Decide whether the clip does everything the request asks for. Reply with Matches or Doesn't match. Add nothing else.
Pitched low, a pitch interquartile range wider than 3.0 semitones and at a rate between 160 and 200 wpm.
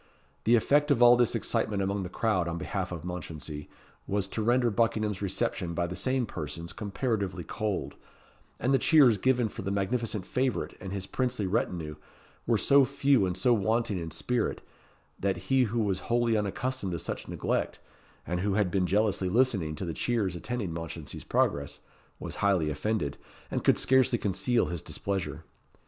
Matches